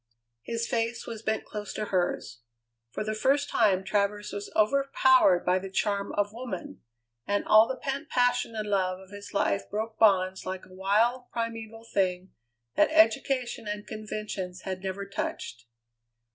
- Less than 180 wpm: Yes, average, 160 wpm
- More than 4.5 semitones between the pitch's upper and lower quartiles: No, average, 3.2 semitones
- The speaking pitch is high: Yes, high, 210 Hz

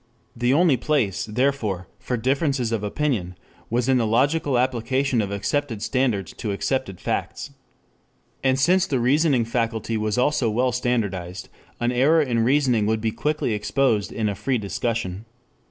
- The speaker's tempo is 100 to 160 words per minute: Yes, average, 155 wpm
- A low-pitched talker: Yes, low, 120 Hz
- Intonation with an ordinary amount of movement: Yes, average, 3.9 semitones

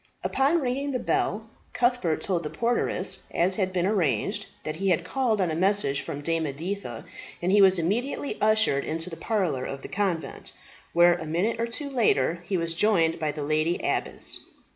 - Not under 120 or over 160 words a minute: No, average, 185 wpm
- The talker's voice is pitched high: No, medium, 180 Hz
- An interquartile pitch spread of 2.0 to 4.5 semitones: No, average, 5.2 semitones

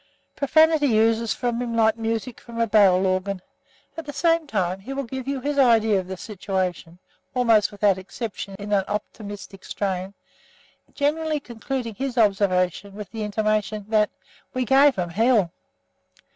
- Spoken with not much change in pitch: No, average, 4.4 semitones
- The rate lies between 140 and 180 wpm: Yes, average, 155 wpm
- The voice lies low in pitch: No, high, 220 Hz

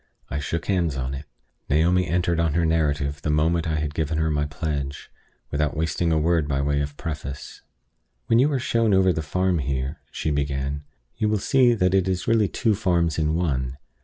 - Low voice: Yes, very low, 80 Hz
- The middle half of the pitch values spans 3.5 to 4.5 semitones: Yes, average, 3.8 semitones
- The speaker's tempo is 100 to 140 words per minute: No, average, 200 wpm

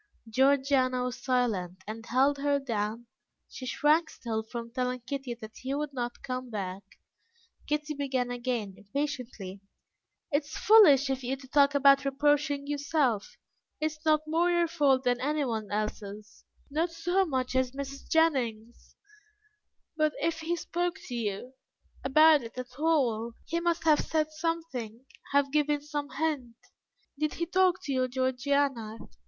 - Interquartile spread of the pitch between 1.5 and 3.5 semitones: No, average, 3.9 semitones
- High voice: Yes, very high, 275 Hz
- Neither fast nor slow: Yes, average, 150 wpm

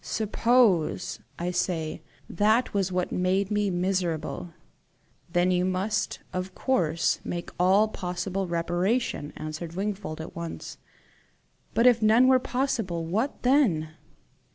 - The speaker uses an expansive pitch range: No, average, 3.8 semitones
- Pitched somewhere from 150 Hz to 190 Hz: Yes, medium, 185 Hz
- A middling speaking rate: No, slow, 120 wpm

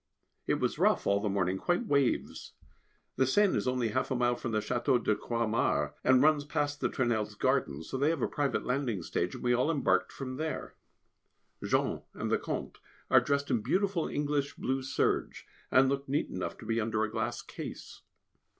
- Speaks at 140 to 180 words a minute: No, average, 195 wpm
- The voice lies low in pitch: Yes, low, 130 Hz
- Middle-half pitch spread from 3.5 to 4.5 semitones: Yes, average, 4.0 semitones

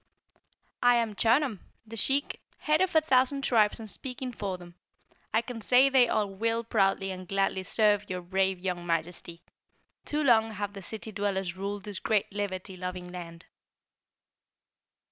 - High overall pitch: Yes, high, 205 Hz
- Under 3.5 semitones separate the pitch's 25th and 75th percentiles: No, average, 3.9 semitones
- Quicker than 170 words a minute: No, average, 160 wpm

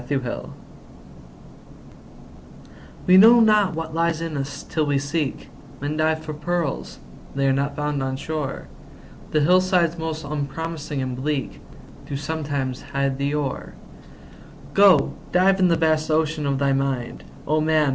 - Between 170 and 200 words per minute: No, average, 145 wpm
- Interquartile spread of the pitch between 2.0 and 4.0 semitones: Yes, average, 2.8 semitones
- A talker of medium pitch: Yes, medium, 150 Hz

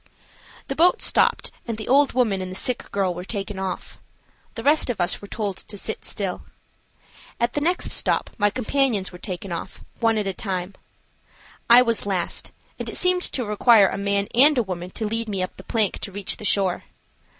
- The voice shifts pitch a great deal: No, average, 4.0 semitones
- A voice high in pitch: Yes, high, 205 Hz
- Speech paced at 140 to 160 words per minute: No, fast, 205 wpm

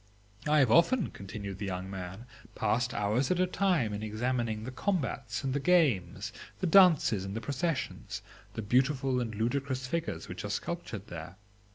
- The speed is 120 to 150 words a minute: No, average, 170 wpm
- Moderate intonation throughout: No, wide, 6.4 semitones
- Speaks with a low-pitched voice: Yes, low, 125 Hz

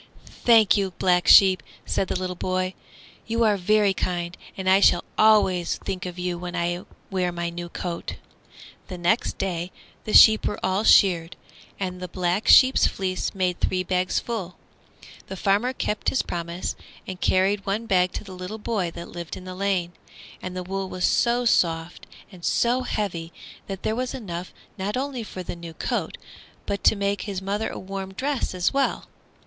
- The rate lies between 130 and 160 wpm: No, average, 180 wpm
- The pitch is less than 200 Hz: Yes, medium, 185 Hz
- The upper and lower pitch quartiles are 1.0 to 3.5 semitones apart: Yes, narrow, 2.6 semitones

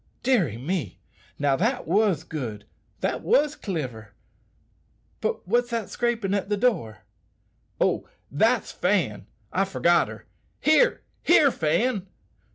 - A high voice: Yes, high, 195 Hz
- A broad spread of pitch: Yes, wide, 8.5 semitones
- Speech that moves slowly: Yes, slow, 120 wpm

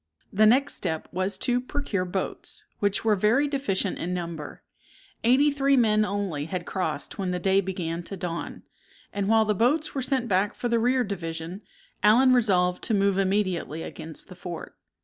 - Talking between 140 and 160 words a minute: No, average, 175 wpm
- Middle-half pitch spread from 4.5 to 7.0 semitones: Yes, average, 4.8 semitones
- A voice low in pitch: No, high, 200 Hz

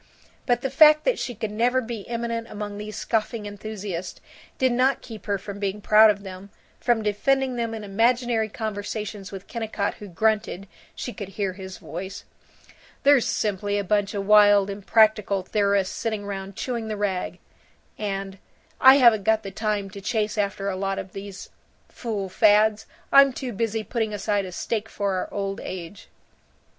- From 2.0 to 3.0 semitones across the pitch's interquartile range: Yes, narrow, 2.4 semitones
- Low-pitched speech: No, high, 210 Hz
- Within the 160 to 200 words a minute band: Yes, average, 170 wpm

